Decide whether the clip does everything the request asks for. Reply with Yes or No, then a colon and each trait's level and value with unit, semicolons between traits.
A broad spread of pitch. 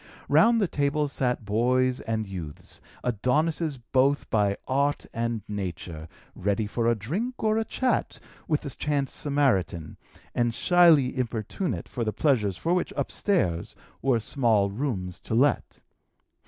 Yes: wide, 5.8 semitones